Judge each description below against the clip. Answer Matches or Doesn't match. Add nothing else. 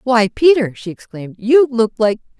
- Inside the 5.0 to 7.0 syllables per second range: Matches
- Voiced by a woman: Matches